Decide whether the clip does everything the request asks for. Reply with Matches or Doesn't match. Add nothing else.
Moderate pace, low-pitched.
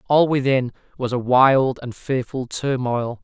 Matches